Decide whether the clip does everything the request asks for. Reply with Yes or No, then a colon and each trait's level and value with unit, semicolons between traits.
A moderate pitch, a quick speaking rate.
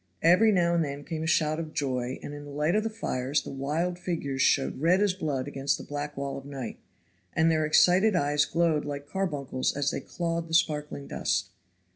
Yes: medium, 150 Hz; fast, 210 wpm